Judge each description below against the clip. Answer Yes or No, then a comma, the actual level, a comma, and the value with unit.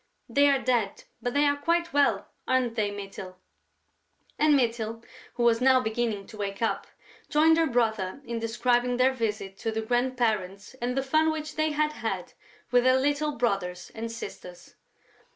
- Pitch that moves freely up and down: No, average, 4.2 semitones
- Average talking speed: Yes, average, 170 wpm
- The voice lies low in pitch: No, high, 245 Hz